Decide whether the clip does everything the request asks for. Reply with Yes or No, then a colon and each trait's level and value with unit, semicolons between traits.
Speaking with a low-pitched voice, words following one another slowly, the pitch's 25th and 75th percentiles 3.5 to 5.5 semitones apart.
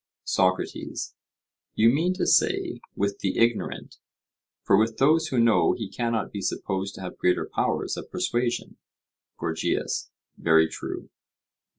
Yes: low, 110 Hz; slow, 130 wpm; average, 3.8 semitones